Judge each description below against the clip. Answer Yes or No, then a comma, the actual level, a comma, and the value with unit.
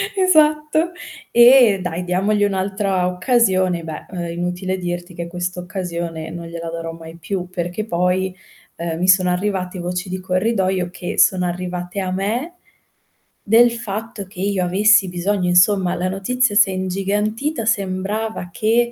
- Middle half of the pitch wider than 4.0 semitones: No, average, 2.8 semitones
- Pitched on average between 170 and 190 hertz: Yes, medium, 185 Hz